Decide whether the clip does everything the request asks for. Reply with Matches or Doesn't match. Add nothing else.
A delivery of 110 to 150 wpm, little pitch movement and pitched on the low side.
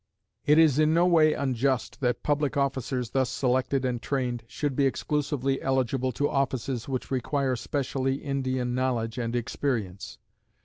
Matches